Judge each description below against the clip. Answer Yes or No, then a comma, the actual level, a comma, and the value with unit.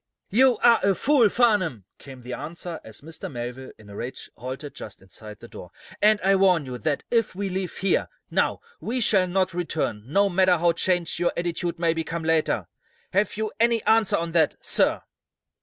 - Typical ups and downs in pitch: No, wide, 6.0 semitones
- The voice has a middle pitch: Yes, medium, 175 Hz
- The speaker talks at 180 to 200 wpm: Yes, average, 185 wpm